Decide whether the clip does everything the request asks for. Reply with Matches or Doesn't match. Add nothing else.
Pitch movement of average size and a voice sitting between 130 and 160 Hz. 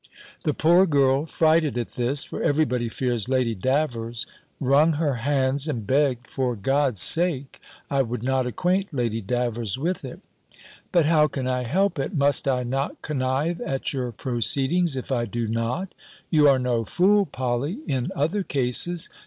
Matches